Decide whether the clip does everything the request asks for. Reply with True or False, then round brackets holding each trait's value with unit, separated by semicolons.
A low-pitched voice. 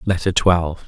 True (90 Hz)